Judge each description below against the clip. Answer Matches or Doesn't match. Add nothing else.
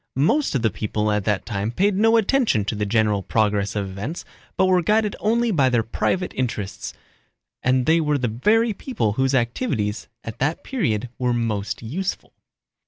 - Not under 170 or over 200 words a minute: Matches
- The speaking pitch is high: Doesn't match